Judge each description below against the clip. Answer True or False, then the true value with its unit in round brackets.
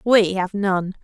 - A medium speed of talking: True (175 wpm)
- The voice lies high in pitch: True (195 Hz)